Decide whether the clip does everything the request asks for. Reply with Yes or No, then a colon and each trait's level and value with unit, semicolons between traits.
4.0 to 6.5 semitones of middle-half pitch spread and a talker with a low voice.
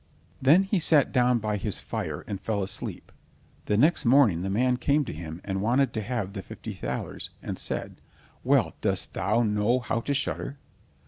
Yes: average, 5.1 semitones; low, 115 Hz